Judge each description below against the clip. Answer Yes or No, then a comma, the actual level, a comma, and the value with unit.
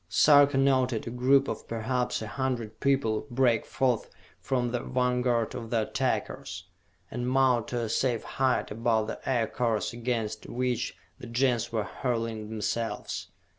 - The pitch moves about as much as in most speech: No, narrow, 2.3 semitones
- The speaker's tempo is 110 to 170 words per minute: Yes, average, 145 wpm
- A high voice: No, low, 120 Hz